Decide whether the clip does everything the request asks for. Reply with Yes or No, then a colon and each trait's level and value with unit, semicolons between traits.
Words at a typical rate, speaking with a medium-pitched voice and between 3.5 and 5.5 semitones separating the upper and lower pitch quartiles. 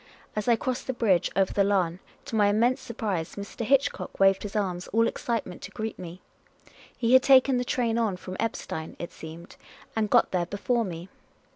No: average, 190 wpm; high, 210 Hz; average, 4.2 semitones